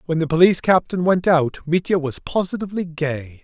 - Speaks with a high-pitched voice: No, medium, 165 Hz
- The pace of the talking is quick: No, average, 175 wpm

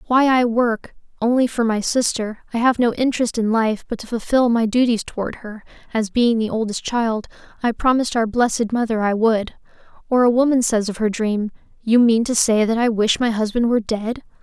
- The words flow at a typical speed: No, fast, 210 wpm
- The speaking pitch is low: No, high, 230 Hz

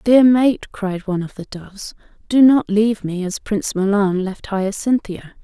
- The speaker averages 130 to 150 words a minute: No, average, 175 wpm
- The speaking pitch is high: Yes, high, 205 Hz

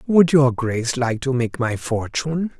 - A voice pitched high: No, low, 130 Hz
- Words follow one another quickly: No, average, 185 wpm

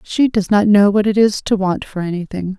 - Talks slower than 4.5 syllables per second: No, 5.2 syllables/s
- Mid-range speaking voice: No, high, 200 Hz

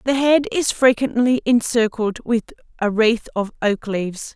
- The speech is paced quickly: No, average, 150 wpm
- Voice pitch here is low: No, high, 230 Hz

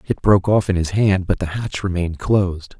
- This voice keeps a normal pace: No, fast, 235 wpm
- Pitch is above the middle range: No, very low, 95 Hz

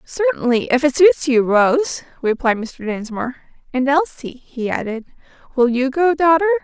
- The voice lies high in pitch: Yes, very high, 275 Hz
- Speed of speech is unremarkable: Yes, average, 155 wpm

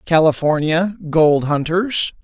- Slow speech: Yes, slow, 80 wpm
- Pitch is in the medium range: Yes, medium, 165 Hz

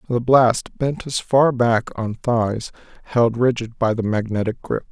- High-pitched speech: No, low, 120 Hz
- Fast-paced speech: No, average, 170 wpm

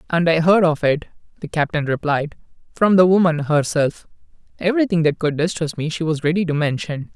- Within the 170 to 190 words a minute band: Yes, average, 185 wpm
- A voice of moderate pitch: Yes, medium, 160 Hz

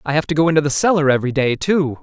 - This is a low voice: No, medium, 150 Hz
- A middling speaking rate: No, fast, 295 wpm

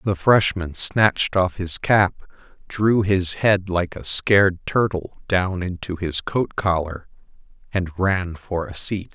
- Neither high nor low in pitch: No, very low, 95 Hz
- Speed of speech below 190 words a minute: Yes, average, 150 wpm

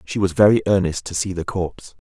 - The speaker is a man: Yes, male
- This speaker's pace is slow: No, fast, 230 wpm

